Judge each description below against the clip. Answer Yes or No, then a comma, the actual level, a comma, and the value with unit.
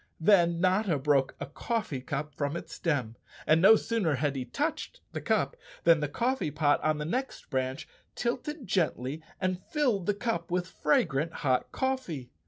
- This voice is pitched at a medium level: Yes, medium, 170 Hz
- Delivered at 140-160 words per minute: No, average, 170 wpm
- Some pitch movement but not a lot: No, wide, 7.5 semitones